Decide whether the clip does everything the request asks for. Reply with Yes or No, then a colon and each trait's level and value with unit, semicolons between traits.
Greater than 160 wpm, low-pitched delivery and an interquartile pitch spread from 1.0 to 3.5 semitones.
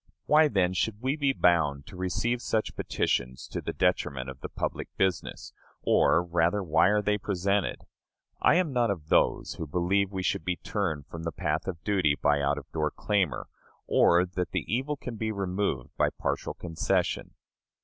No: average, 180 wpm; very low, 90 Hz; average, 4.5 semitones